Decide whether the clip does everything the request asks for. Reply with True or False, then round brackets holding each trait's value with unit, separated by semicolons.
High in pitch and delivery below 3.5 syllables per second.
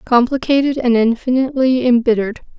False (245 Hz; 5.9 syllables/s)